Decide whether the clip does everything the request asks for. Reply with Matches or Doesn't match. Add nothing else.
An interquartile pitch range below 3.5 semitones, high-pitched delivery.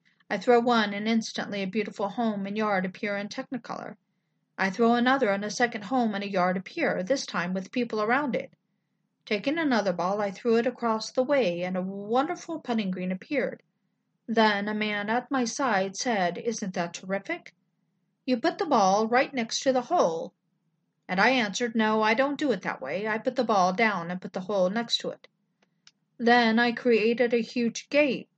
Doesn't match